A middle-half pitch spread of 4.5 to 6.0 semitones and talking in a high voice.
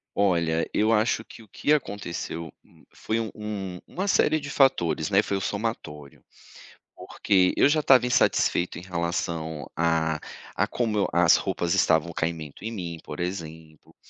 No: average, 5.1 semitones; very low, 90 Hz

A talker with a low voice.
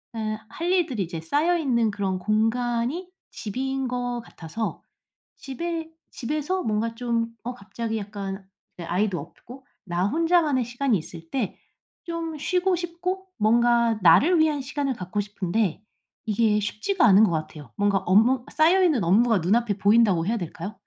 No: high, 230 Hz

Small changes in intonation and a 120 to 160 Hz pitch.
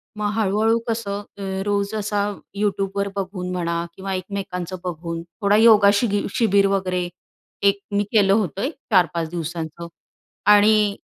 No: narrow, 2.3 semitones; high, 200 Hz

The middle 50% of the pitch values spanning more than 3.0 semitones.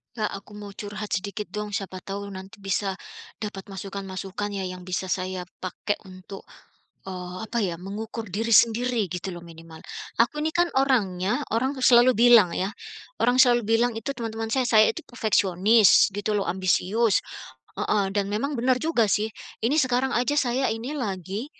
Yes: average, 3.9 semitones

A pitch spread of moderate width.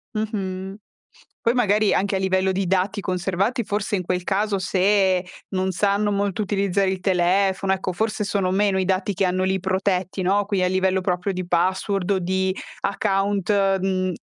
No: narrow, 1.3 semitones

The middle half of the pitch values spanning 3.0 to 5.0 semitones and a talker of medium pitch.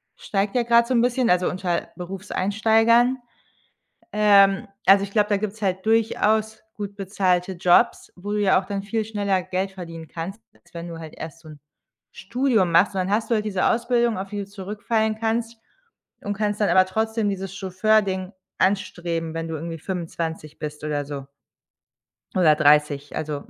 No: average, 3.8 semitones; high, 195 Hz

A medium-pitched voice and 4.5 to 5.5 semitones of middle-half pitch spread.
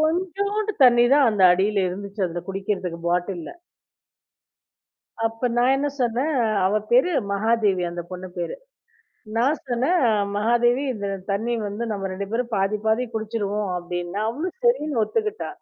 No: high, 225 Hz; average, 5.0 semitones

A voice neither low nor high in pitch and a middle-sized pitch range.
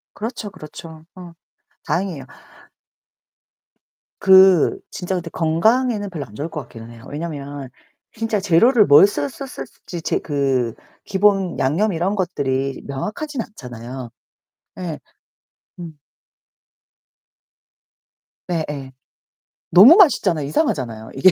No: medium, 165 Hz; wide, 6.2 semitones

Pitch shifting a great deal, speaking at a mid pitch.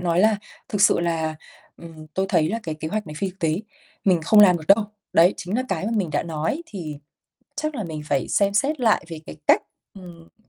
No: average, 4.4 semitones; medium, 180 Hz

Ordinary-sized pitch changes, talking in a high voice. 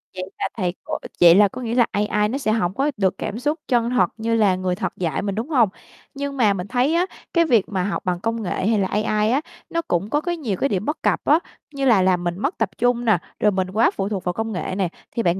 Yes: average, 4.9 semitones; high, 215 Hz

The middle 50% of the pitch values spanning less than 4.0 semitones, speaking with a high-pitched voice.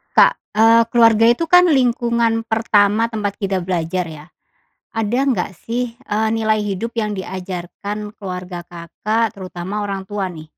Yes: average, 3.5 semitones; high, 210 Hz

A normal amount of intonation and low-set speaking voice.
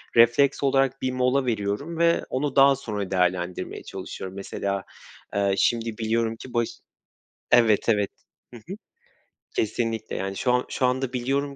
Yes: average, 4.5 semitones; low, 120 Hz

